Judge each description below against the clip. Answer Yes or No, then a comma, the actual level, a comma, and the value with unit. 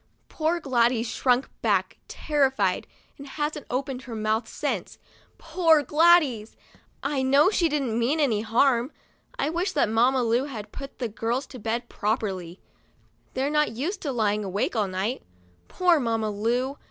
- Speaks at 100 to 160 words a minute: Yes, average, 155 wpm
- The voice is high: Yes, very high, 255 Hz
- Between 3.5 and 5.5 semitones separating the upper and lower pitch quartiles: Yes, average, 4.7 semitones